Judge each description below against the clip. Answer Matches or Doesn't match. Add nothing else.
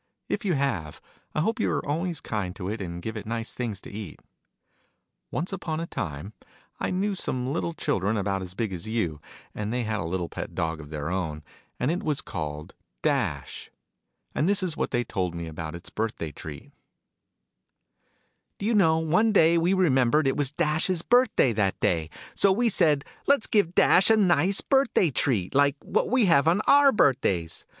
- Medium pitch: Doesn't match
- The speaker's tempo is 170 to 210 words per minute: Matches